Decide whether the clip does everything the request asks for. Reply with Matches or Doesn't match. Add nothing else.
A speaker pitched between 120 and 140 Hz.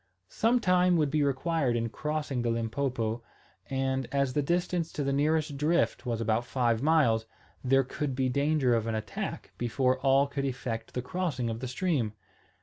Matches